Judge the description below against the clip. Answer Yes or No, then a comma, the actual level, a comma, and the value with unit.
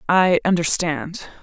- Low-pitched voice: No, medium, 170 Hz